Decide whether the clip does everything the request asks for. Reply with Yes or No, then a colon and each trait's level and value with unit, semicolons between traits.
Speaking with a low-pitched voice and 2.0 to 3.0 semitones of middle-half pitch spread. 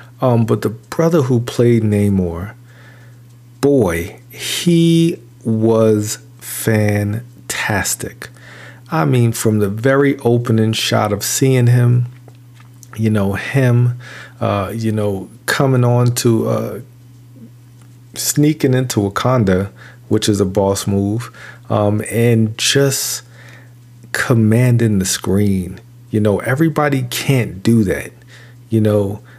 Yes: low, 120 Hz; narrow, 2.4 semitones